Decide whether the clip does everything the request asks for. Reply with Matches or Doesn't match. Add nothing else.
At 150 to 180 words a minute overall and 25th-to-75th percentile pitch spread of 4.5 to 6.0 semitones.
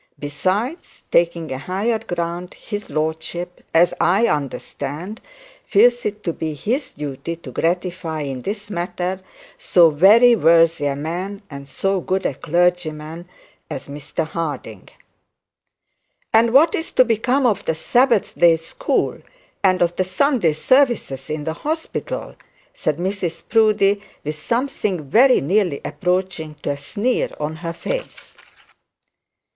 Doesn't match